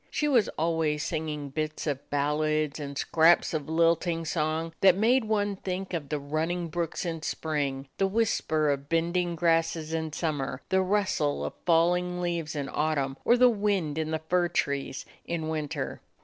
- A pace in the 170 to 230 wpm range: Yes, average, 175 wpm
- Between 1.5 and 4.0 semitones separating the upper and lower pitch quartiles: Yes, average, 2.8 semitones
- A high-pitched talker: No, medium, 160 Hz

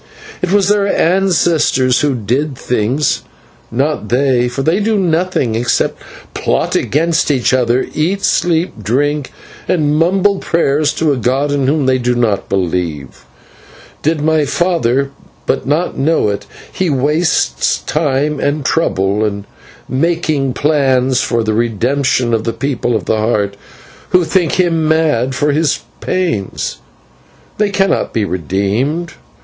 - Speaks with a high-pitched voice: No, medium, 140 Hz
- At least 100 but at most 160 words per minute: Yes, average, 140 wpm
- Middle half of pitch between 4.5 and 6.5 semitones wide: Yes, average, 5.3 semitones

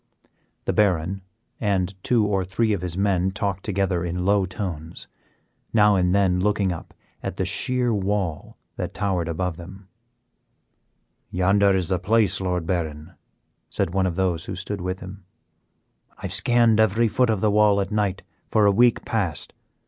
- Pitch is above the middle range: No, very low, 95 Hz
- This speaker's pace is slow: No, average, 165 wpm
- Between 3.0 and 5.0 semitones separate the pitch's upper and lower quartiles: No, narrow, 2.4 semitones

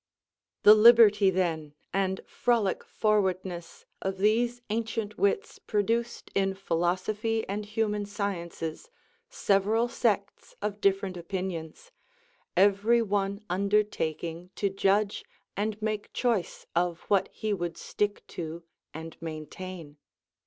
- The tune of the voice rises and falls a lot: No, average, 3.0 semitones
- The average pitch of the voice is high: Yes, high, 200 Hz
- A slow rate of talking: Yes, slow, 110 wpm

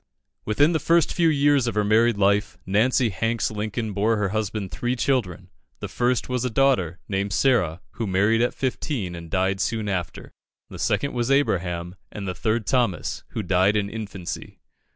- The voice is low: Yes, low, 110 Hz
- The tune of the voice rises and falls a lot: No, average, 4.2 semitones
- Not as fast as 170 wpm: No, average, 175 wpm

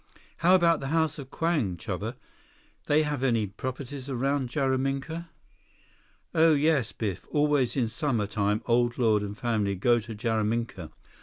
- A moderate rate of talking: Yes, average, 145 wpm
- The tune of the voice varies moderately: Yes, average, 4.9 semitones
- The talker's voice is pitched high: No, low, 130 Hz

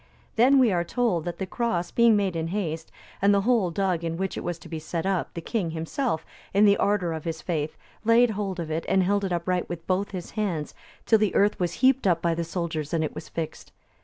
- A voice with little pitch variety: No, average, 3.7 semitones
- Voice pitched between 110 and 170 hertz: No, medium, 180 Hz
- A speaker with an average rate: No, fast, 245 wpm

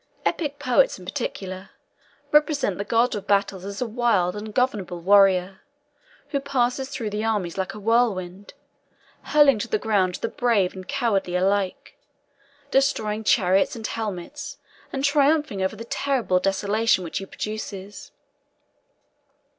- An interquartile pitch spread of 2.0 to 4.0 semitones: No, average, 4.6 semitones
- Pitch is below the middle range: No, high, 210 Hz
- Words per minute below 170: Yes, slow, 135 wpm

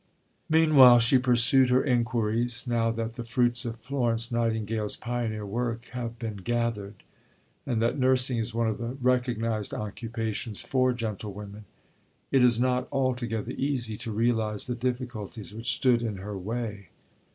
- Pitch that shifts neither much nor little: No, narrow, 2.0 semitones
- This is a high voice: No, low, 115 Hz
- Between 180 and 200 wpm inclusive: No, average, 145 wpm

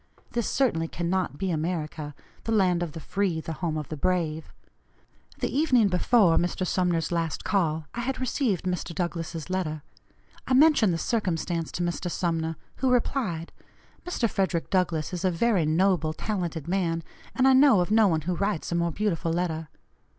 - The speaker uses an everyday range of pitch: Yes, average, 3.8 semitones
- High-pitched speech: No, medium, 175 Hz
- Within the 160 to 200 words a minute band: Yes, average, 170 wpm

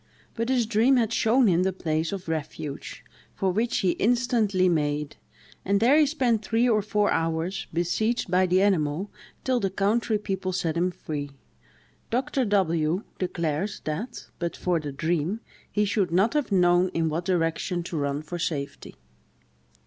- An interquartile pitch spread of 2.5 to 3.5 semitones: No, average, 5.0 semitones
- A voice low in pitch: No, medium, 185 Hz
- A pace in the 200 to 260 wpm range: No, average, 165 wpm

